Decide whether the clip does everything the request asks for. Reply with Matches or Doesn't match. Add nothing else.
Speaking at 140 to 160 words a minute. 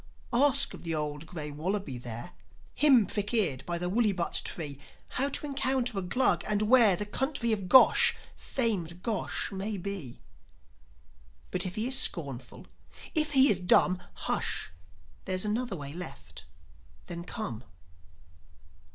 Matches